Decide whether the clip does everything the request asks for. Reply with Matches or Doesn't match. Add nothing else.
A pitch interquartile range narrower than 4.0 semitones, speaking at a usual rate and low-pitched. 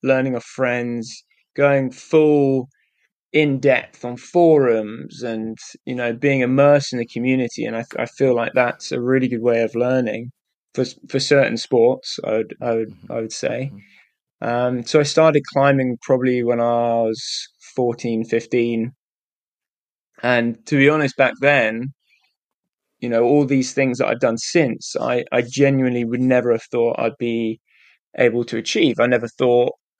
Matches